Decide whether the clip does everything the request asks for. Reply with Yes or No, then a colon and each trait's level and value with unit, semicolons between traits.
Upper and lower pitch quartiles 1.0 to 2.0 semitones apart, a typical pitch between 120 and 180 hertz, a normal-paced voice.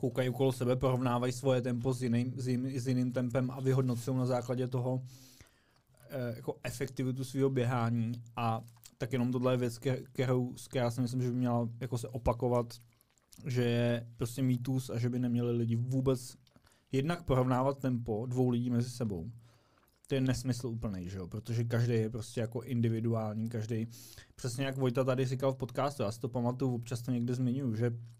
No: narrow, 1.7 semitones; low, 125 Hz; fast, 180 wpm